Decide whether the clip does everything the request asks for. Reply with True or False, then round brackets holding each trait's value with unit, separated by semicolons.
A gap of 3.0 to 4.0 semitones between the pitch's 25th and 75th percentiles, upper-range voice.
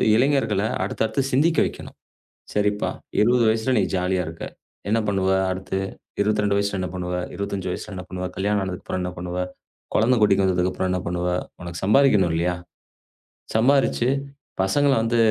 False (3.5 semitones; 100 Hz)